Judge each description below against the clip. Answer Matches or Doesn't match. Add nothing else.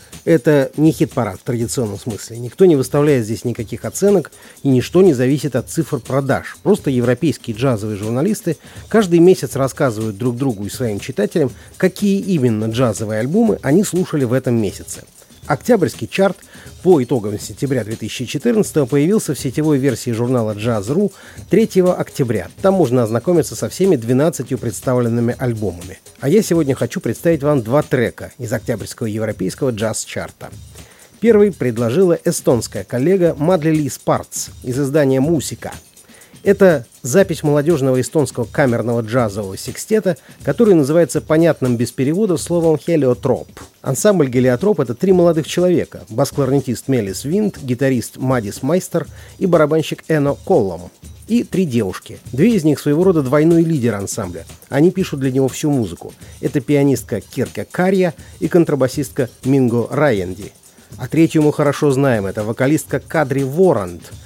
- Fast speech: Doesn't match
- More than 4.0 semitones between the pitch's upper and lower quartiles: Matches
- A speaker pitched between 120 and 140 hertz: Matches